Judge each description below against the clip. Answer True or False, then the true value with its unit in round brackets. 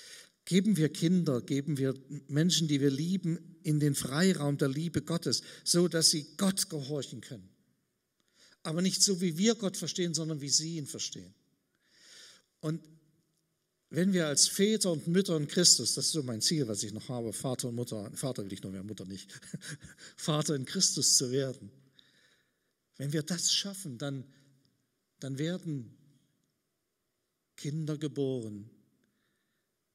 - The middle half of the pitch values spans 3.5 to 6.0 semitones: True (4.2 semitones)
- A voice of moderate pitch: True (150 Hz)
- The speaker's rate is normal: True (150 wpm)